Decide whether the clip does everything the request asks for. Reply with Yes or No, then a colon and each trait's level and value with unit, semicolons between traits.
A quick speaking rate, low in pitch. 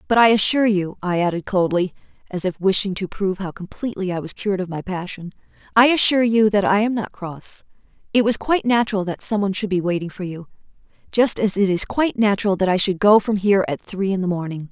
No: fast, 230 wpm; high, 195 Hz